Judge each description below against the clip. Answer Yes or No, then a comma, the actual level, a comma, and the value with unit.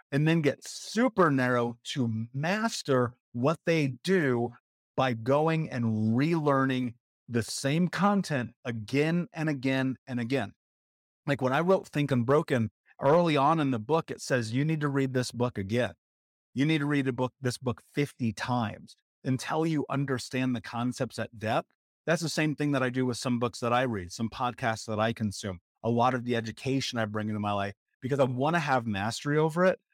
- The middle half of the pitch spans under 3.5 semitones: No, average, 3.9 semitones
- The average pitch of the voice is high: No, low, 130 Hz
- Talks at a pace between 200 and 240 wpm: No, average, 190 wpm